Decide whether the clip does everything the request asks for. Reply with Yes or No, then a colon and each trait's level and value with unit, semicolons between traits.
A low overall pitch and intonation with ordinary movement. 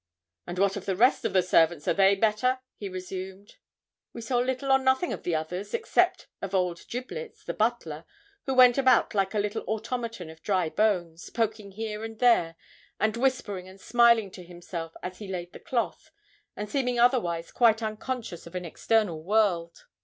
No: high, 205 Hz; average, 4.7 semitones